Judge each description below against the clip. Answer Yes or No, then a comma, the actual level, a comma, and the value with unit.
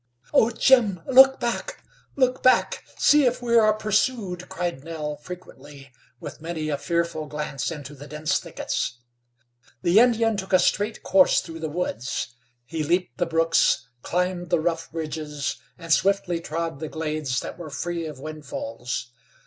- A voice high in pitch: No, medium, 165 Hz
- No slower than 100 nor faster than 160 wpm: Yes, average, 155 wpm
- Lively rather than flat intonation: No, average, 4.5 semitones